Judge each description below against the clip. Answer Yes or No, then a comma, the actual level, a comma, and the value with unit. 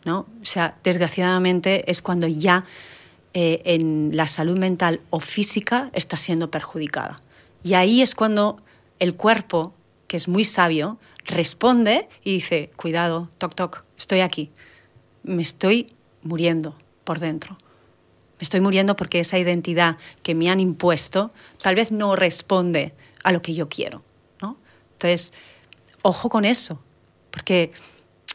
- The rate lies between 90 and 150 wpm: Yes, average, 140 wpm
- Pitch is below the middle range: No, medium, 175 Hz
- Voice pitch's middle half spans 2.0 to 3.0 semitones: Yes, narrow, 2.5 semitones